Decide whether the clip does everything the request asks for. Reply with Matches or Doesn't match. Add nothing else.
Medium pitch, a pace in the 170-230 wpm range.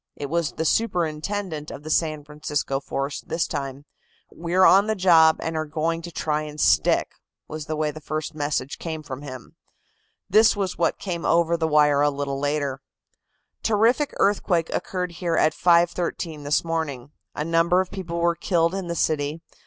Matches